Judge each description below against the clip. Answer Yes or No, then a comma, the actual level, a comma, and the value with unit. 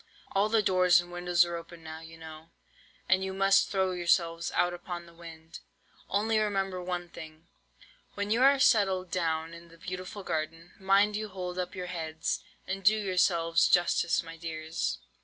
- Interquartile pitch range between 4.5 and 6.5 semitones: No, narrow, 2.5 semitones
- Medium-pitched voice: Yes, medium, 175 Hz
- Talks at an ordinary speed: Yes, average, 175 wpm